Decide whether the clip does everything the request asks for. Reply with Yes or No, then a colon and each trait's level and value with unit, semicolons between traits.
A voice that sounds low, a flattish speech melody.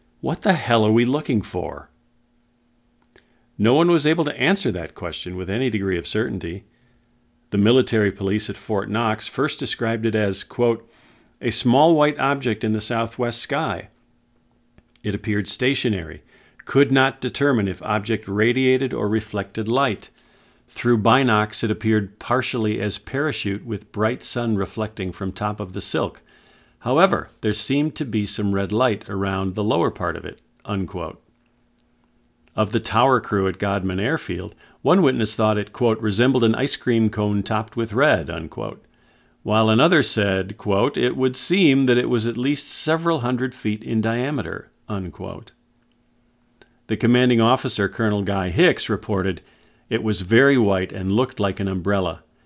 No: low, 110 Hz; average, 3.5 semitones